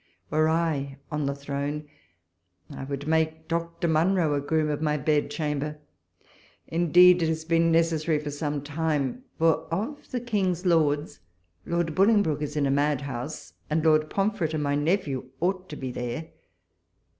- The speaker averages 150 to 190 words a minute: Yes, average, 160 wpm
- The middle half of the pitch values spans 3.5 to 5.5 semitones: No, narrow, 2.5 semitones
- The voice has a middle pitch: Yes, medium, 155 Hz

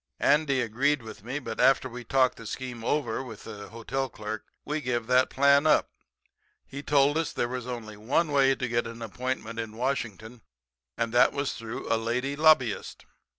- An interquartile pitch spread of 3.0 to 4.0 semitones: Yes, average, 3.4 semitones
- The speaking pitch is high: No, low, 125 Hz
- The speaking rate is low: No, average, 190 wpm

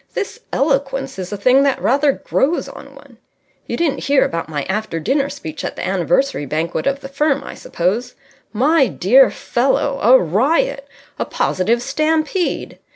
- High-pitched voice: Yes, very high, 270 Hz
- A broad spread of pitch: Yes, wide, 6.3 semitones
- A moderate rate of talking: Yes, average, 160 wpm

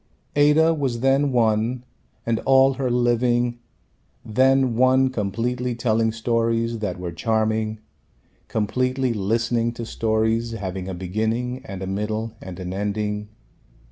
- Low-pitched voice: Yes, low, 115 Hz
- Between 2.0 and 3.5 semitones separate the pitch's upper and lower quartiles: Yes, average, 2.7 semitones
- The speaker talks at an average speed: No, slow, 125 wpm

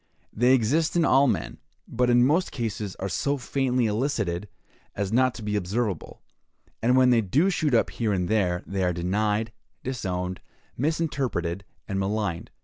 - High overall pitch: No, low, 110 Hz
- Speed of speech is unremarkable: Yes, average, 160 wpm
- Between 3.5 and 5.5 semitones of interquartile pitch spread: Yes, average, 5.0 semitones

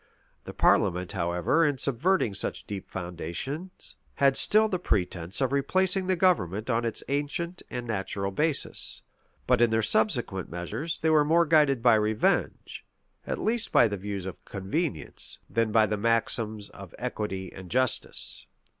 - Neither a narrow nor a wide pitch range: No, wide, 7.7 semitones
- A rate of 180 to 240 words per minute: No, average, 155 wpm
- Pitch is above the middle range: No, low, 115 Hz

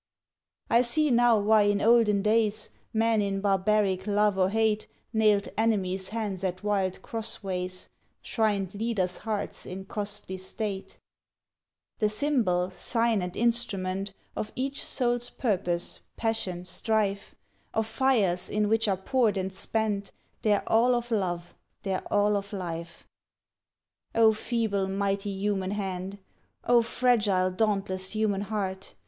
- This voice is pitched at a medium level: No, high, 205 Hz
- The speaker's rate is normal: No, slow, 130 wpm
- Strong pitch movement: No, average, 2.7 semitones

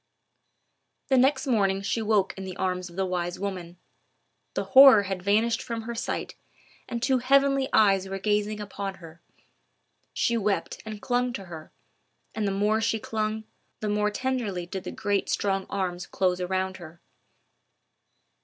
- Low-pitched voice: No, high, 205 Hz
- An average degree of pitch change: Yes, average, 3.1 semitones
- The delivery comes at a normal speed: Yes, average, 160 wpm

